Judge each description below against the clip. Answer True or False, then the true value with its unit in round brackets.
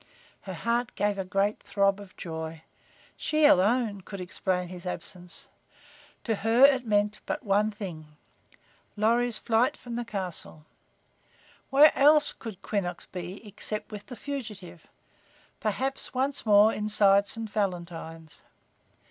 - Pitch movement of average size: True (4.1 semitones)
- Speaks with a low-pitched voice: False (205 Hz)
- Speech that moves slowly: True (130 wpm)